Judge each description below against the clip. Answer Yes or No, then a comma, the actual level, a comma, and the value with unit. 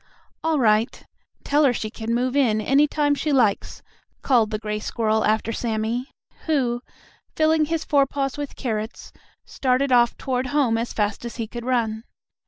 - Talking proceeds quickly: No, average, 165 wpm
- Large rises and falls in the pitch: No, average, 4.2 semitones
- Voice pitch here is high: Yes, high, 245 Hz